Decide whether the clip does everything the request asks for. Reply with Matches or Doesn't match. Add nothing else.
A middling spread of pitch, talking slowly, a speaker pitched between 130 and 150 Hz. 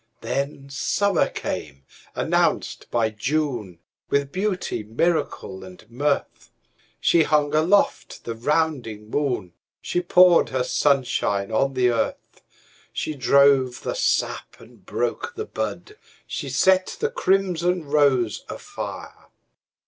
Doesn't match